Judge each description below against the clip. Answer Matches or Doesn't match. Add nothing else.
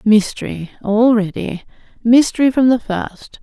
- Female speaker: Matches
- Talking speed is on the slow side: Matches